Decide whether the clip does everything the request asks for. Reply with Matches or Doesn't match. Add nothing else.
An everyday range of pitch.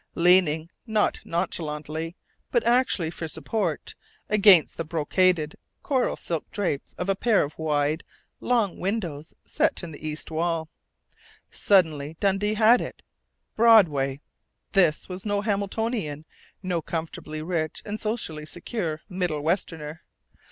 Matches